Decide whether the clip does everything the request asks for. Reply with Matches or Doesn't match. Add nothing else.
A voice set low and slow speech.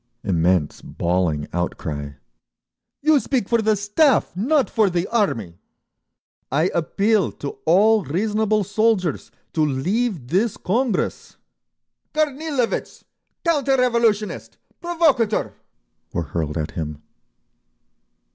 Doesn't match